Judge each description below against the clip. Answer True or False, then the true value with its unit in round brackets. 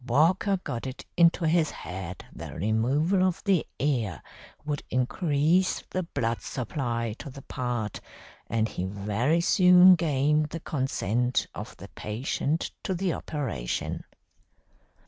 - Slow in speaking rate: True (125 wpm)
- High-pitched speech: False (140 Hz)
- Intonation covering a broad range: True (6.4 semitones)